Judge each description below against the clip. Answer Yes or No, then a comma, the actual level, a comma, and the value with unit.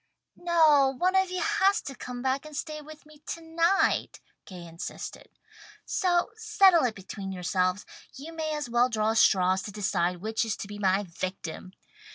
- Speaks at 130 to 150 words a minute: No, average, 175 wpm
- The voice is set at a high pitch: Yes, very high, 260 Hz